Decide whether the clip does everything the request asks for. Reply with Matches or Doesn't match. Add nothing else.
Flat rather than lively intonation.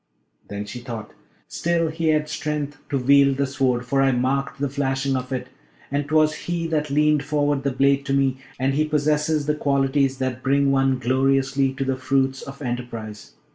Matches